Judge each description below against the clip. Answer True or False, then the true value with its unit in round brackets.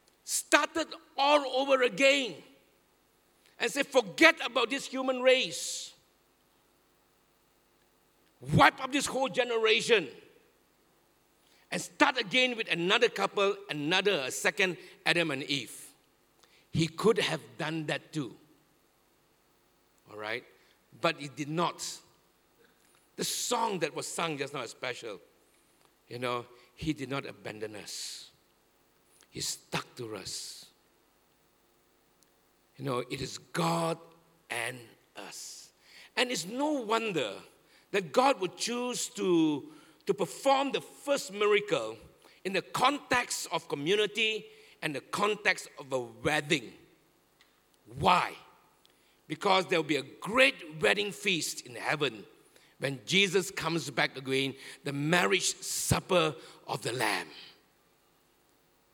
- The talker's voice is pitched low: False (185 Hz)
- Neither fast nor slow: False (115 wpm)